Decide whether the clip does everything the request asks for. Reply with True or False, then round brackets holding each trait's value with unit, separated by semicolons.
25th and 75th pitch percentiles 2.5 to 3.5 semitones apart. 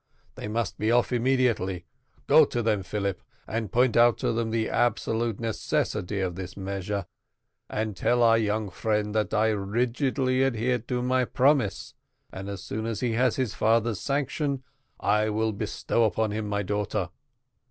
True (2.8 semitones)